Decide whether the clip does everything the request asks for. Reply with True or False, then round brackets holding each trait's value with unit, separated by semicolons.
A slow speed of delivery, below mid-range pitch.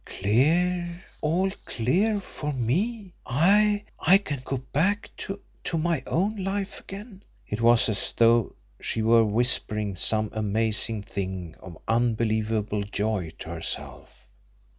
True (125 wpm; 125 Hz)